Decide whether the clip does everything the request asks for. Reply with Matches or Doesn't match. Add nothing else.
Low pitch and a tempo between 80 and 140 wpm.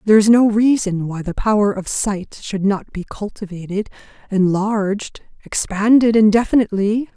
Doesn't match